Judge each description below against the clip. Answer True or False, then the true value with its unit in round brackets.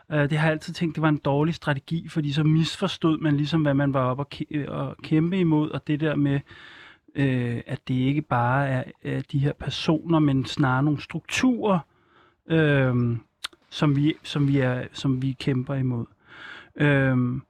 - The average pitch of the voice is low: False (145 Hz)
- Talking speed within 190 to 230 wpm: False (160 wpm)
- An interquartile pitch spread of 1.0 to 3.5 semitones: True (2.8 semitones)